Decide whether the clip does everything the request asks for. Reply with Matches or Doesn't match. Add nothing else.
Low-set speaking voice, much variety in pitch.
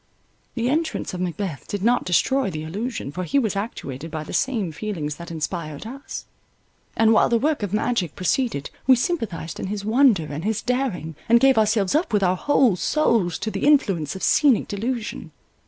Doesn't match